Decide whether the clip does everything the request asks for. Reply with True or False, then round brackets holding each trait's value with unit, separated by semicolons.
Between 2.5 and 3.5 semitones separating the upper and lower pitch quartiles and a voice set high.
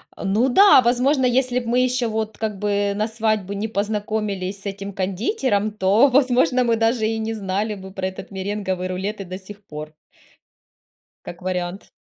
True (3.2 semitones; 210 Hz)